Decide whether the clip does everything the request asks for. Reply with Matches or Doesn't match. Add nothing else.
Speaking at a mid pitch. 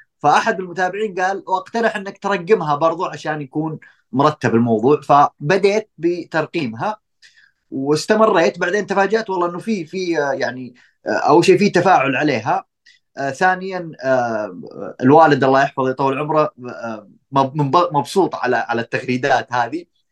Matches